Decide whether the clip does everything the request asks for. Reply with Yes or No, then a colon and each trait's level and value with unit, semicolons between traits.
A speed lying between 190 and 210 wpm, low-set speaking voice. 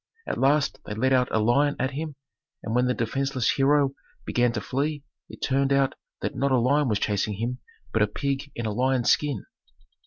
Yes: fast, 205 wpm; low, 130 Hz